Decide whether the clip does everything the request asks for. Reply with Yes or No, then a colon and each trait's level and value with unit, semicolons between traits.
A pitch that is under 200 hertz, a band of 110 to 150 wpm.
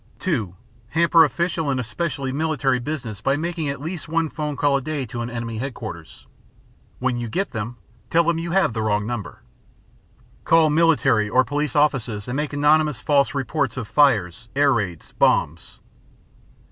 No: medium, 140 Hz; average, 165 wpm